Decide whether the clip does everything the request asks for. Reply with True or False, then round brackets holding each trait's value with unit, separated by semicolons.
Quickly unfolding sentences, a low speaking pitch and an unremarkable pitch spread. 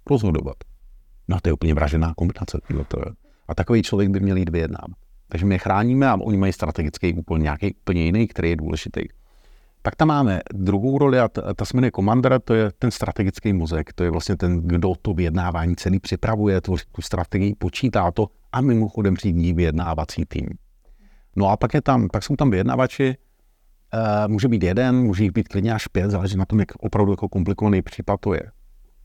True (190 wpm; 100 Hz; 4.1 semitones)